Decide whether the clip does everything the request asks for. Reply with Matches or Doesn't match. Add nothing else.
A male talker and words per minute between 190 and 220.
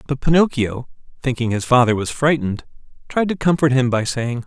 Doesn't match